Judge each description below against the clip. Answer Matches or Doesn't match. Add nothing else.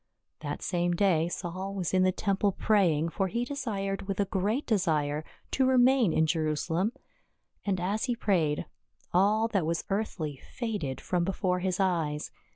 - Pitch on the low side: Doesn't match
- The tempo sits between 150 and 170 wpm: Matches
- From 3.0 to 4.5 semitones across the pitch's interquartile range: Matches